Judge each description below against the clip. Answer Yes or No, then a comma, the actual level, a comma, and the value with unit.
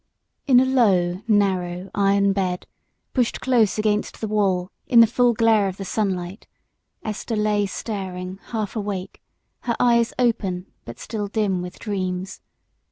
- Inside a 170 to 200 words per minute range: No, average, 150 wpm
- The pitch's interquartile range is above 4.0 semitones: No, average, 3.2 semitones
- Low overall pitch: No, high, 205 Hz